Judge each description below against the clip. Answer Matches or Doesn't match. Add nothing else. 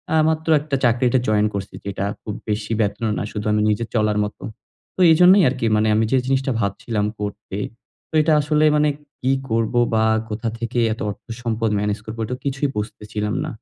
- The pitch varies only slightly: Doesn't match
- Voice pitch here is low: Matches